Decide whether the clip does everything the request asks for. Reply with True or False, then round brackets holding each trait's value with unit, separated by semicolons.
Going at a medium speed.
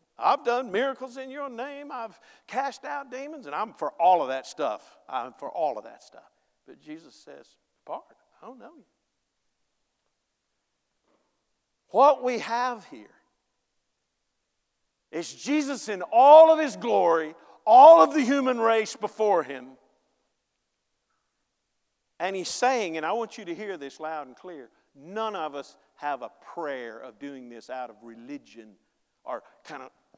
True (155 wpm)